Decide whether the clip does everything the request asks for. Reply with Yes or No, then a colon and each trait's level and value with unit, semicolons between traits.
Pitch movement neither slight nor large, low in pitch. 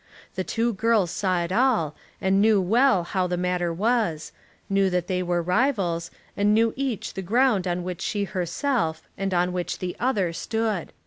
No: average, 4.0 semitones; high, 190 Hz